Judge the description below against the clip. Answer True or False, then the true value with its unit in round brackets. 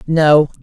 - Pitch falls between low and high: True (150 Hz)